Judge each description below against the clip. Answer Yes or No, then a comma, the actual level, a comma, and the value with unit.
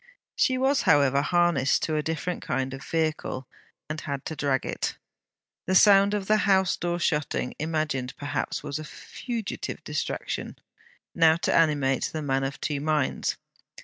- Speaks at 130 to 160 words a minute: Yes, average, 155 wpm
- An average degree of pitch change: Yes, average, 4.0 semitones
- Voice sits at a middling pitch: Yes, medium, 155 Hz